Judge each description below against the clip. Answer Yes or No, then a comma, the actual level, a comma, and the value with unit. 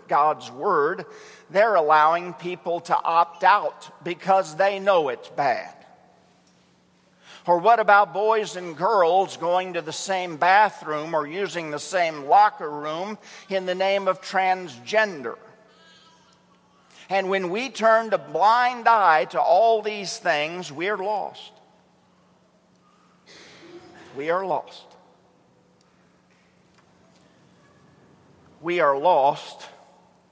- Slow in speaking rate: Yes, slow, 110 wpm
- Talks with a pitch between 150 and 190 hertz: Yes, medium, 185 Hz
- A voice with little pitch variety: No, average, 3.8 semitones